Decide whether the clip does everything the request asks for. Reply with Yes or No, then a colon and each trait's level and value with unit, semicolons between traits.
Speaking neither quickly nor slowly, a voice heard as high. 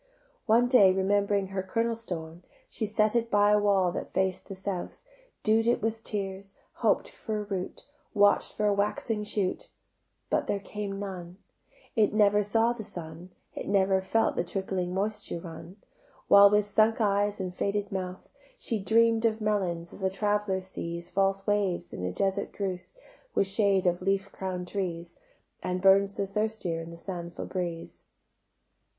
Yes: average, 165 wpm; high, 195 Hz